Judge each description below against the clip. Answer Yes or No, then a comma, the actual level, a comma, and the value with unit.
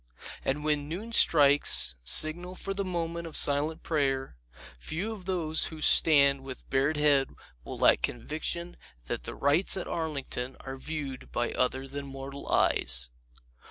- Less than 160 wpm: Yes, average, 150 wpm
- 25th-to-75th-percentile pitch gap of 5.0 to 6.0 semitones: No, average, 3.5 semitones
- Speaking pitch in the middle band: Yes, medium, 145 Hz